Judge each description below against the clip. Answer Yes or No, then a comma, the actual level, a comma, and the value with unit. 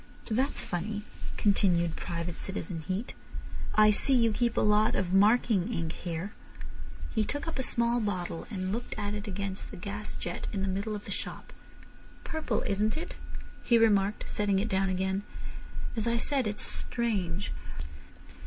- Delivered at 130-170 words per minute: Yes, average, 160 wpm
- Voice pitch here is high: Yes, high, 205 Hz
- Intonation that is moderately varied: Yes, average, 3.2 semitones